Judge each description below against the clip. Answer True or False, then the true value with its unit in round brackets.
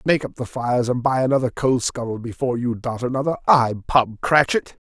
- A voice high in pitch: False (125 Hz)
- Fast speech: False (195 wpm)